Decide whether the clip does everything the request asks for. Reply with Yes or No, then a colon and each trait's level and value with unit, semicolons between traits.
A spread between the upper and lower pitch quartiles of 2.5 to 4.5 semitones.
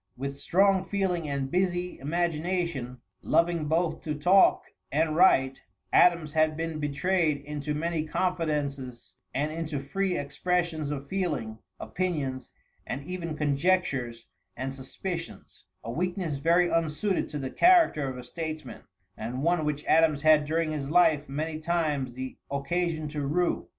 Yes: average, 3.8 semitones